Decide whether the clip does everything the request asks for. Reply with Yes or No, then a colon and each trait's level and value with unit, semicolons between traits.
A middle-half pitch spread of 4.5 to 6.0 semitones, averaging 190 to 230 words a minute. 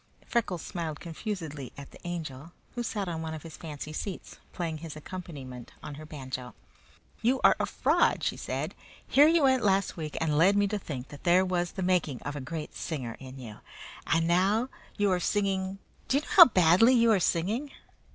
Yes: average, 4.9 semitones; average, 200 wpm